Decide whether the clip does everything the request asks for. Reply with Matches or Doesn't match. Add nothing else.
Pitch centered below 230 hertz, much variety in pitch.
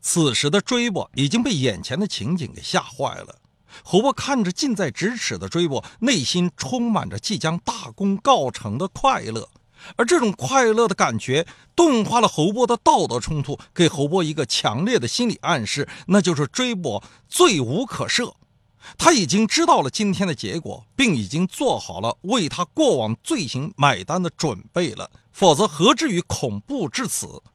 Matches